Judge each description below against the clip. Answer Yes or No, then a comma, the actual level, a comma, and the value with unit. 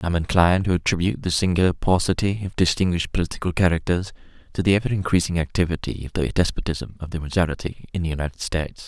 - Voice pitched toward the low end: Yes, very low, 85 Hz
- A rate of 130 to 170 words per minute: No, average, 180 wpm